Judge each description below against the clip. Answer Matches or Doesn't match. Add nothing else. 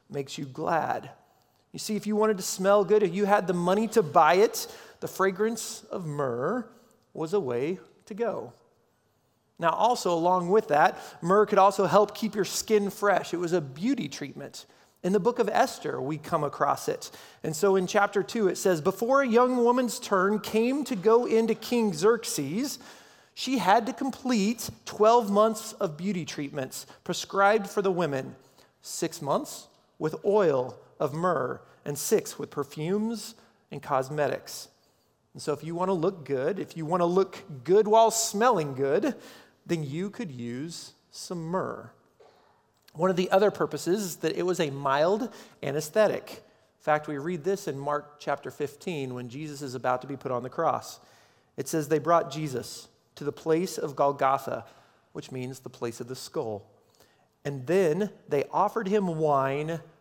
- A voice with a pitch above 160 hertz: Matches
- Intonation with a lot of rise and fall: Matches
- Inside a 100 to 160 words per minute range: Doesn't match